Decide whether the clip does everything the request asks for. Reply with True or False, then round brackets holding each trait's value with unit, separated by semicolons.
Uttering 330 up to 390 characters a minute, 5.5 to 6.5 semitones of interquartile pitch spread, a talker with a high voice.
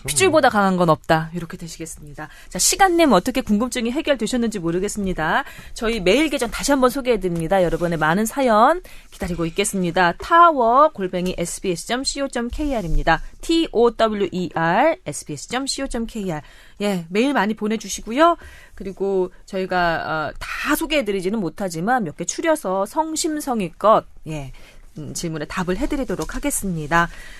False (350 characters per minute; 7.0 semitones; 200 Hz)